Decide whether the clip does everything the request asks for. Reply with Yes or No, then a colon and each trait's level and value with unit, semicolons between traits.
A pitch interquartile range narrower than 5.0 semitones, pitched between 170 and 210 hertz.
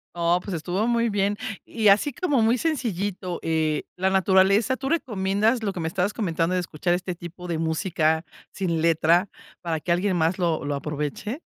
Yes: average, 3.8 semitones; medium, 185 Hz